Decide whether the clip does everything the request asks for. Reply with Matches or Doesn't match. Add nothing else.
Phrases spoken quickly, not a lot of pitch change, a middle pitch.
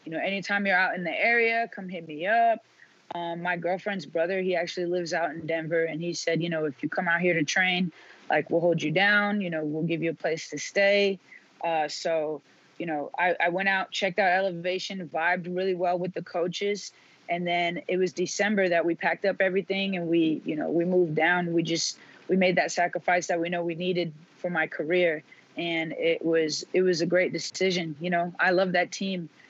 Matches